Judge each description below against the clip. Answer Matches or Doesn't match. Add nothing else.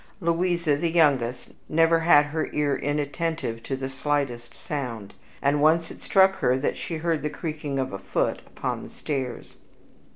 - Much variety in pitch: Doesn't match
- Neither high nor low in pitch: Matches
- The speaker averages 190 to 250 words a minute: Doesn't match